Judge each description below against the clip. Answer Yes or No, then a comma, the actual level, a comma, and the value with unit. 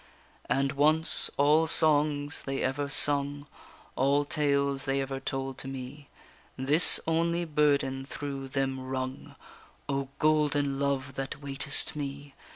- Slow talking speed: Yes, slow, 125 wpm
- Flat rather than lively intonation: Yes, narrow, 1.5 semitones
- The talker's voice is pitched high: No, medium, 140 Hz